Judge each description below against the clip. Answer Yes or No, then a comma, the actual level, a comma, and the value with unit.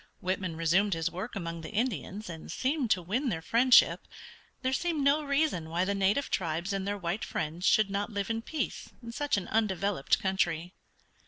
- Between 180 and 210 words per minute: Yes, average, 185 wpm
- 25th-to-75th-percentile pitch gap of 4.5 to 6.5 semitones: Yes, average, 5.1 semitones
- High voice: Yes, high, 200 Hz